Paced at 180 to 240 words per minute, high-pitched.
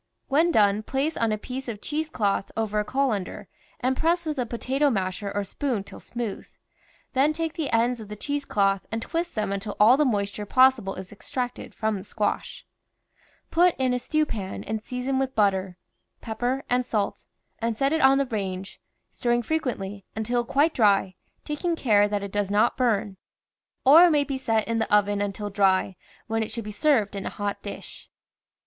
Yes: average, 200 wpm; high, 225 Hz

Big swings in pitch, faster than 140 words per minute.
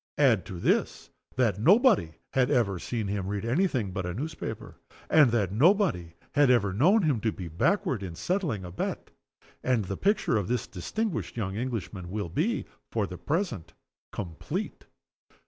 Yes: wide, 8.0 semitones; average, 165 wpm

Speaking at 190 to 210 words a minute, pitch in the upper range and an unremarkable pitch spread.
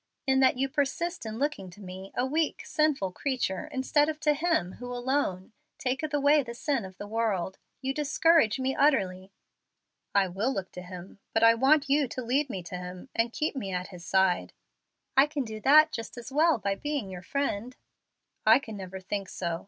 No: average, 200 wpm; high, 245 Hz; wide, 6.8 semitones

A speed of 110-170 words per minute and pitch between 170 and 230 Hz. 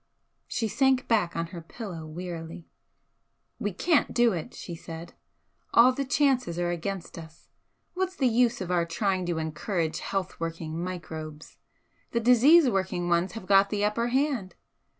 Yes: average, 155 wpm; medium, 185 Hz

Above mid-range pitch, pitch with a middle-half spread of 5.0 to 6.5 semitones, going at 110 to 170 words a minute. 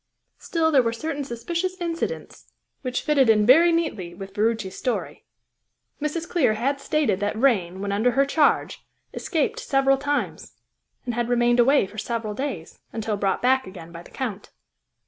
Yes: high, 245 Hz; wide, 5.5 semitones; average, 165 wpm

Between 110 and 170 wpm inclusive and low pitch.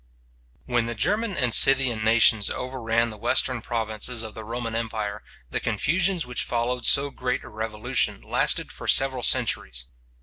Yes: average, 155 wpm; low, 115 Hz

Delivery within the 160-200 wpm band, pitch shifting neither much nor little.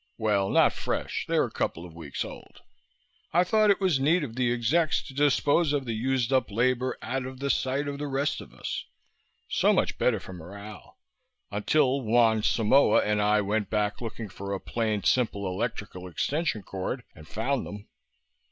Yes: average, 180 wpm; average, 4.8 semitones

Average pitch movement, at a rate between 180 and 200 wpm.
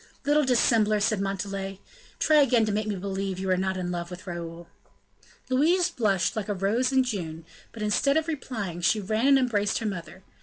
Yes: average, 4.8 semitones; average, 195 wpm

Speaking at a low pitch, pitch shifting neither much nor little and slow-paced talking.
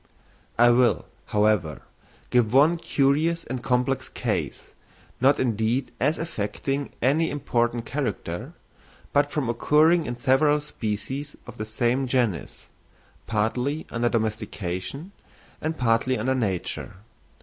Yes: low, 125 Hz; average, 4.4 semitones; slow, 115 wpm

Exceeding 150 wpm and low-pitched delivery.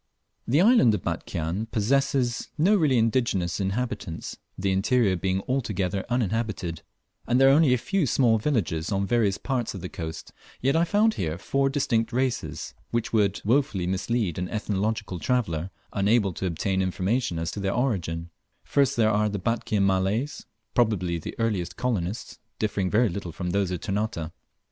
Yes: average, 165 wpm; low, 105 Hz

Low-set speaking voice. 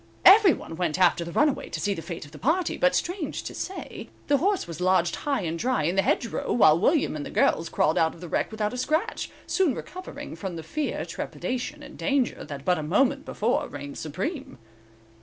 No: high, 210 Hz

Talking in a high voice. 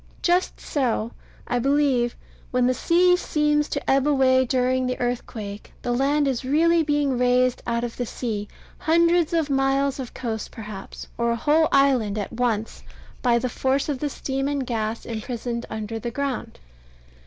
Yes: very high, 255 Hz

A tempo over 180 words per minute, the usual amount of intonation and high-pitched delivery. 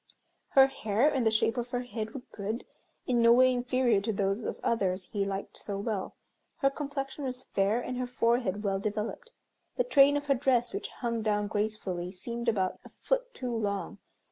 Yes: average, 195 wpm; average, 3.8 semitones; high, 235 Hz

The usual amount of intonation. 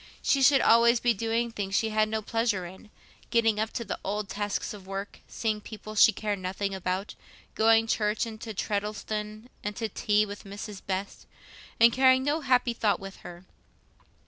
No: narrow, 2.2 semitones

